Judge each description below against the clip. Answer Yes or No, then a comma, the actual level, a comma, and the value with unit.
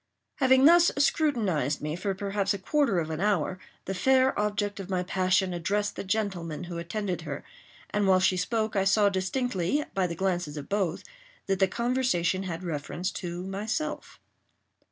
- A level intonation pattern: No, average, 3.1 semitones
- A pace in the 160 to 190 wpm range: Yes, average, 170 wpm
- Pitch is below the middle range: No, high, 195 Hz